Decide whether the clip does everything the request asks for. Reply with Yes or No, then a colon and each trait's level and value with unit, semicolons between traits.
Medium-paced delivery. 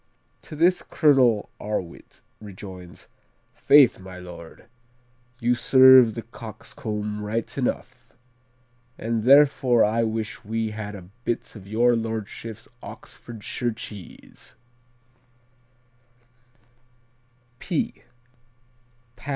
No: slow, 85 wpm